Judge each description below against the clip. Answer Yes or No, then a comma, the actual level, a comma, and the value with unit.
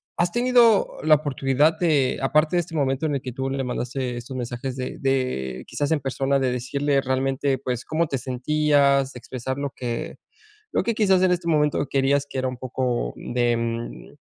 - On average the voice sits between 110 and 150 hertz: Yes, low, 135 Hz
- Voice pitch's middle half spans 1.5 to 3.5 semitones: Yes, average, 2.9 semitones